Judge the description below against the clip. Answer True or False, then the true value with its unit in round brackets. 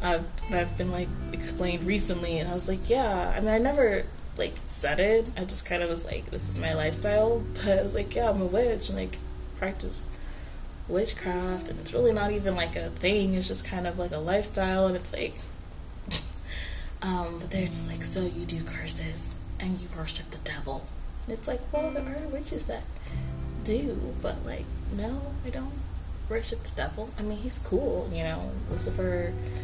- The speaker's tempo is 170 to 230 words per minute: True (195 wpm)